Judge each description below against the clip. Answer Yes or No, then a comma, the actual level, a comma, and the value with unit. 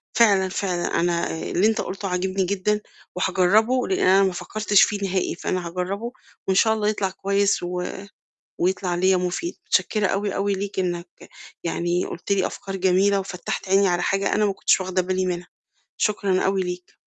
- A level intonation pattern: Yes, narrow, 1.8 semitones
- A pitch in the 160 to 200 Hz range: Yes, high, 190 Hz